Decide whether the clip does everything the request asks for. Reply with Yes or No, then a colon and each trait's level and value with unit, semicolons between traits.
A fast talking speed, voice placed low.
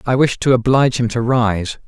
Yes: fast, 225 wpm; low, 120 Hz